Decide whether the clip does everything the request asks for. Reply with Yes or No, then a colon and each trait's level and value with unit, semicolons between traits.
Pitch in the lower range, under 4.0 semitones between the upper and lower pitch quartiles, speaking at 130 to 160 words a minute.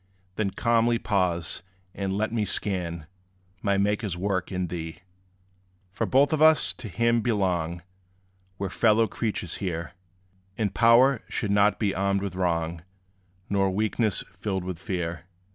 Yes: low, 100 Hz; average, 3.5 semitones; average, 145 wpm